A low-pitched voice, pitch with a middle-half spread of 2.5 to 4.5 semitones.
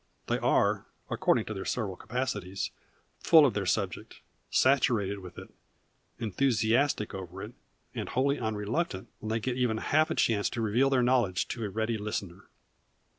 Yes: low, 110 Hz; average, 4.0 semitones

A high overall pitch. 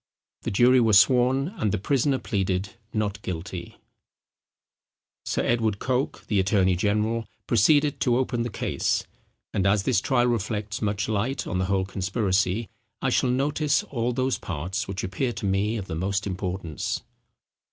No: low, 105 Hz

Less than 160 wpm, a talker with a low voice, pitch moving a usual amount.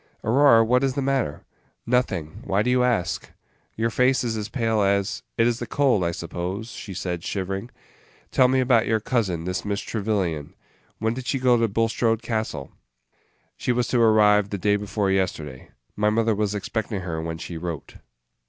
No: average, 185 wpm; low, 110 Hz; average, 4.0 semitones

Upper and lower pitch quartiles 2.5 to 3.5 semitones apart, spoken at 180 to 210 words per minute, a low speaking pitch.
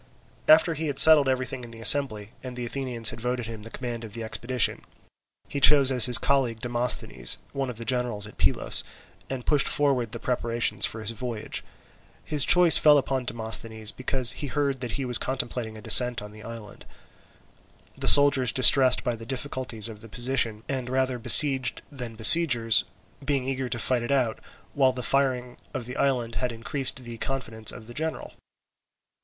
Yes: average, 2.8 semitones; average, 185 wpm; low, 125 Hz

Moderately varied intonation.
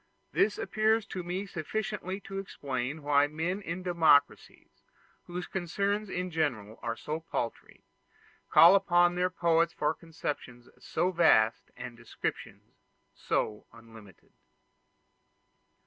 Yes: average, 4.5 semitones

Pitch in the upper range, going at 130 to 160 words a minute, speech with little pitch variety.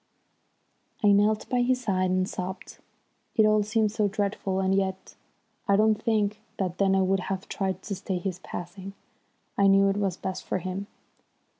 No: high, 195 Hz; average, 175 wpm; narrow, 1.8 semitones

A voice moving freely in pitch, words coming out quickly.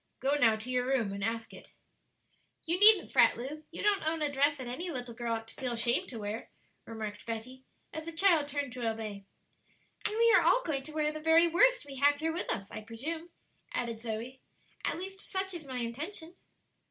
Yes: wide, 6.0 semitones; fast, 215 wpm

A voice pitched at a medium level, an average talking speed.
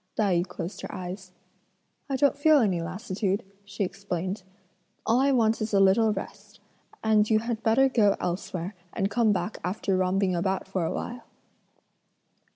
No: high, 200 Hz; average, 165 wpm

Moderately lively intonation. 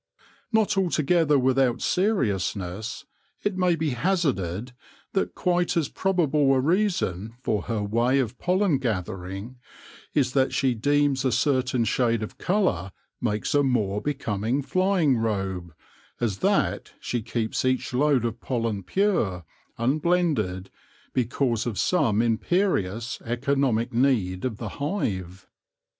No: wide, 5.8 semitones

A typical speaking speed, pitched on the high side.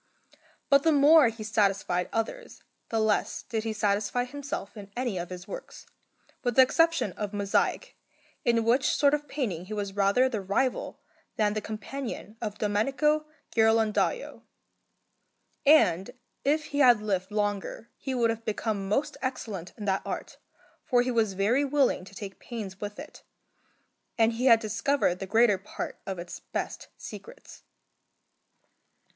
Yes: average, 150 wpm; high, 220 Hz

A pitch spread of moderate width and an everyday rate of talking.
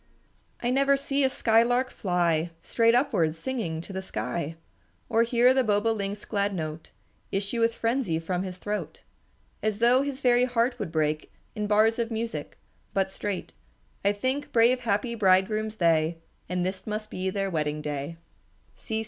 Yes: average, 4.7 semitones; average, 155 wpm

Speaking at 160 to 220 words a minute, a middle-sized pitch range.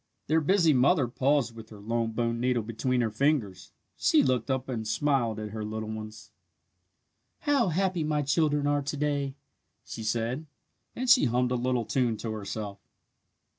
Yes: average, 170 wpm; average, 4.6 semitones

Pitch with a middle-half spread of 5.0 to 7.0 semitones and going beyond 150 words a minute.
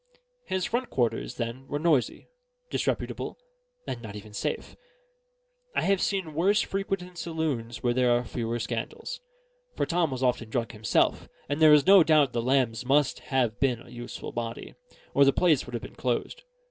Yes: wide, 5.4 semitones; average, 170 wpm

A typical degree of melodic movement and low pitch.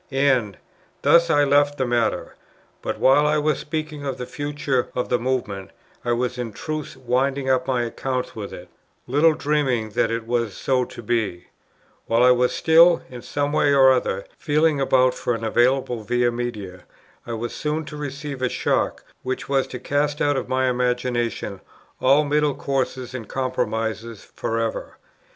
Yes: average, 3.2 semitones; low, 130 Hz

